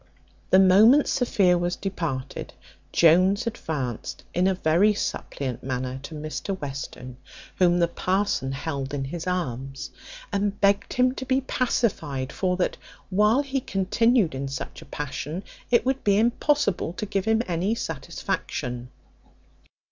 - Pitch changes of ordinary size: No, wide, 6.8 semitones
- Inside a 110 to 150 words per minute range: Yes, average, 140 wpm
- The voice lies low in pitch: No, medium, 180 Hz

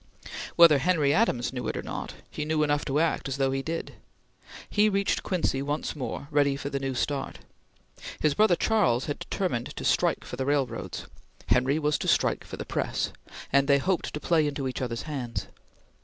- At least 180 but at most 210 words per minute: Yes, average, 195 wpm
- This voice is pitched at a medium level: Yes, medium, 145 Hz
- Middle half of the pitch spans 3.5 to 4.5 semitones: No, average, 3.1 semitones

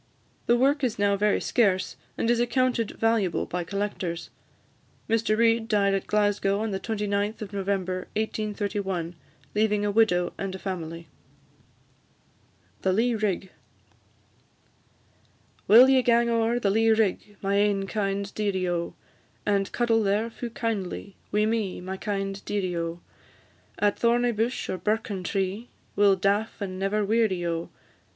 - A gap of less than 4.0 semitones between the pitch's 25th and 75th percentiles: Yes, narrow, 2.6 semitones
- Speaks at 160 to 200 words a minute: No, average, 145 wpm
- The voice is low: No, high, 205 Hz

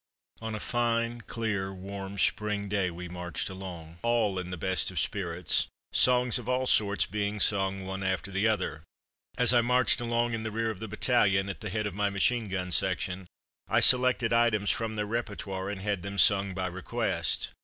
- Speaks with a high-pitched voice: No, low, 100 Hz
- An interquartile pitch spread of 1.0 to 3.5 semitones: Yes, average, 3.2 semitones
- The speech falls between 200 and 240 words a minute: No, average, 190 wpm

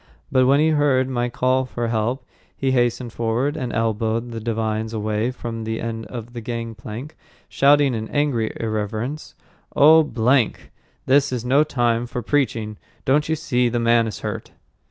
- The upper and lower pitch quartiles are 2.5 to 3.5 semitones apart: Yes, average, 2.9 semitones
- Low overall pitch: Yes, low, 120 Hz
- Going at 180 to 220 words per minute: No, average, 165 wpm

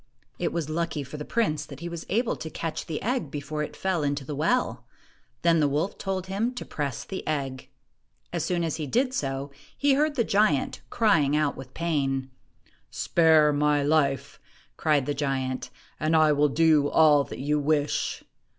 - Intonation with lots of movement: No, average, 3.1 semitones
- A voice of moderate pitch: Yes, medium, 155 Hz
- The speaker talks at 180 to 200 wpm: Yes, average, 185 wpm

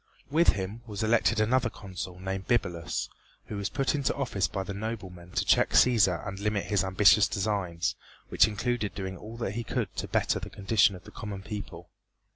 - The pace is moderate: Yes, average, 190 wpm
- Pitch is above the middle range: No, low, 100 Hz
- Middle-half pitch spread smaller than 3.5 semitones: Yes, average, 2.8 semitones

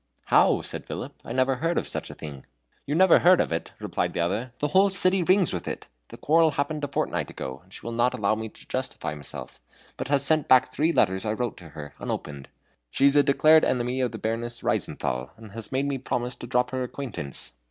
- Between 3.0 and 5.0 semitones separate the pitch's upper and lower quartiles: No, wide, 5.4 semitones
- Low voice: Yes, low, 125 Hz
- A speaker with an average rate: No, fast, 230 wpm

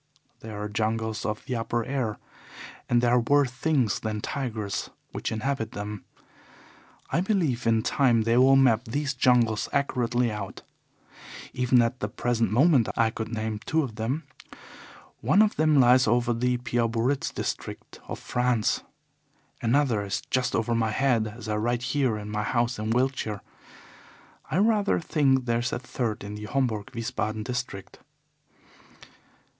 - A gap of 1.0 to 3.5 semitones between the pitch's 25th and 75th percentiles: Yes, average, 3.1 semitones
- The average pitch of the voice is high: No, low, 120 Hz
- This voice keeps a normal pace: Yes, average, 155 wpm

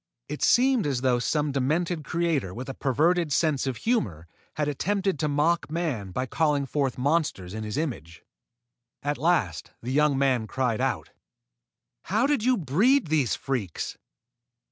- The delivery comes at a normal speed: Yes, average, 155 wpm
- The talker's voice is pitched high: No, medium, 145 Hz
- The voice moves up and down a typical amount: Yes, average, 5.0 semitones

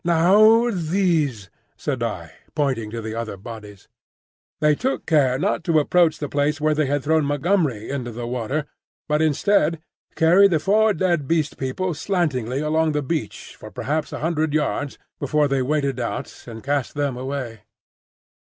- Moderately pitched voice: Yes, medium, 150 Hz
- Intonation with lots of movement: No, average, 4.2 semitones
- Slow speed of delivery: No, average, 160 wpm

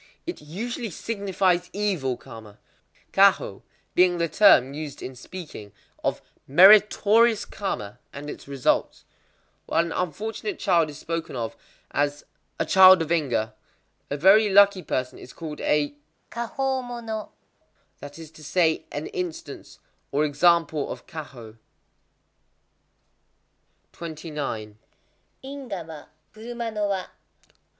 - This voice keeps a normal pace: No, slow, 115 wpm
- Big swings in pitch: Yes, wide, 5.9 semitones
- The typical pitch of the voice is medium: Yes, medium, 165 Hz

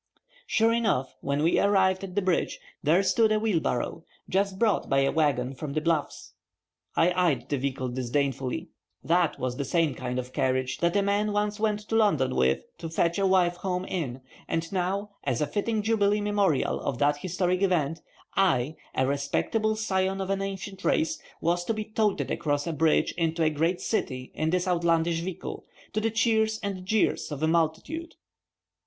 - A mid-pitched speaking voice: Yes, medium, 175 Hz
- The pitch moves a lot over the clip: Yes, wide, 5.7 semitones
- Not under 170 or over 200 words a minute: Yes, average, 185 wpm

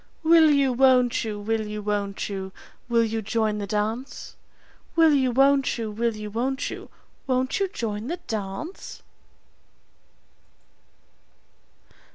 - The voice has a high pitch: Yes, high, 230 Hz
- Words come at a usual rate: No, slow, 130 wpm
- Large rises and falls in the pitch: No, average, 4.2 semitones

